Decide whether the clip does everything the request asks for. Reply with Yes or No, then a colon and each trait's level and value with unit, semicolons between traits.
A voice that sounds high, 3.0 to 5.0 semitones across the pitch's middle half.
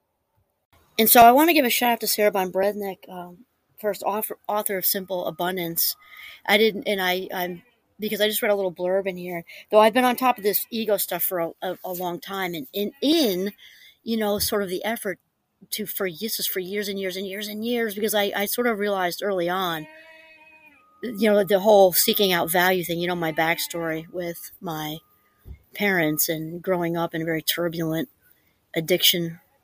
Yes: high, 195 Hz; average, 3.4 semitones